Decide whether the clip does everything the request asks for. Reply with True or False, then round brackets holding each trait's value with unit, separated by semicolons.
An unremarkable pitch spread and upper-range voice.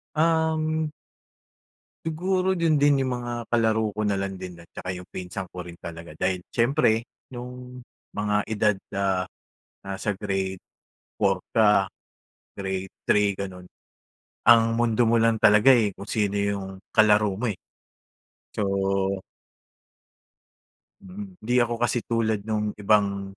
False (3.9 semitones; 110 Hz)